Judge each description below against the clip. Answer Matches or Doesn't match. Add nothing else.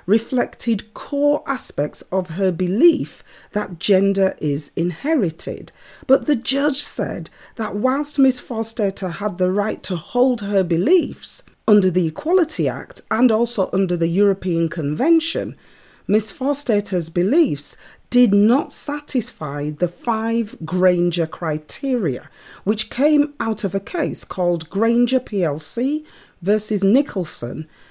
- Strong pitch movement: Matches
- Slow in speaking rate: Matches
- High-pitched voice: Matches